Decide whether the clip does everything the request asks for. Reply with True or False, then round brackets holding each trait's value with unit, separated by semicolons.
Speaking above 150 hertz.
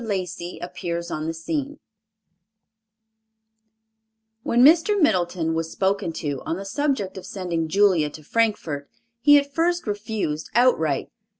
True (190 Hz)